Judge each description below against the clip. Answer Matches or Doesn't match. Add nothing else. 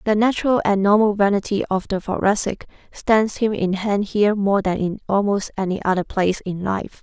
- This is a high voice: Matches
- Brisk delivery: Doesn't match